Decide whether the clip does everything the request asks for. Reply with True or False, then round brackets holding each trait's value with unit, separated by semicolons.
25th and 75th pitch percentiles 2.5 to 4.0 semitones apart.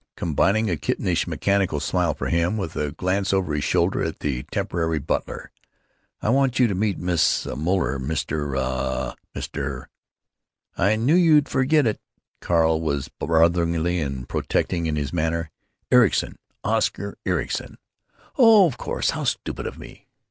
False (5.1 semitones)